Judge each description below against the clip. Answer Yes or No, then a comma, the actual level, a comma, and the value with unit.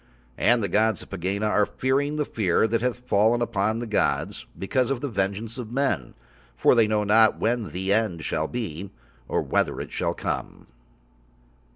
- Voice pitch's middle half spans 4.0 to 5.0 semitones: No, average, 3.3 semitones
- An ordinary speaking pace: Yes, average, 180 wpm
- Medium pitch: No, low, 110 Hz